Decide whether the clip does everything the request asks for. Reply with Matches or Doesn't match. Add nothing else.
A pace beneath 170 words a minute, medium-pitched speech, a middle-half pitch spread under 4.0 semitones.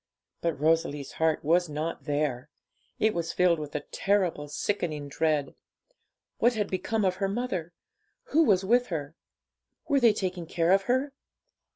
Doesn't match